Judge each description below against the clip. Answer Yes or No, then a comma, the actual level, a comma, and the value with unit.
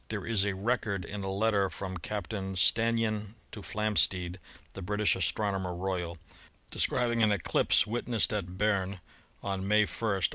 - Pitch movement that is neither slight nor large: No, narrow, 2.2 semitones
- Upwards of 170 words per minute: No, average, 155 wpm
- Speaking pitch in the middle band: No, low, 100 Hz